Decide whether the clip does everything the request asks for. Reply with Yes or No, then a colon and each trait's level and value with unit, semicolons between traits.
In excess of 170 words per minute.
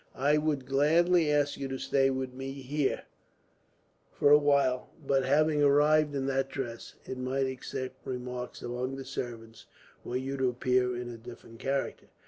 No: average, 165 wpm